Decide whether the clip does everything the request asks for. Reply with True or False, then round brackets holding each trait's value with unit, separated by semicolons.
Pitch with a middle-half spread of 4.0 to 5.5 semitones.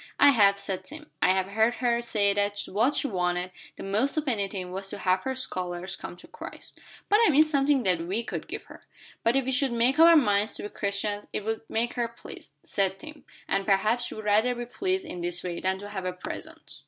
True (4.8 semitones)